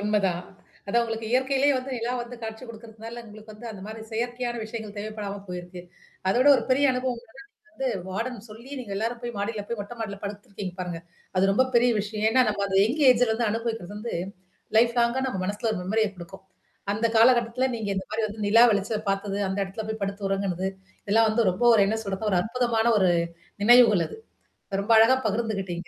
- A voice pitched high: Yes, high, 220 Hz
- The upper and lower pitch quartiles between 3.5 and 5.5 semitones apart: No, average, 2.9 semitones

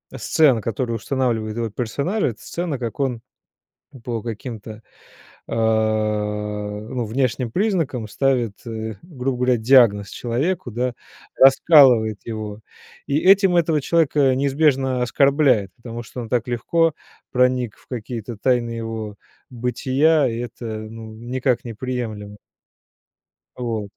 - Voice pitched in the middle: No, low, 125 Hz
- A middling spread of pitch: Yes, average, 3.3 semitones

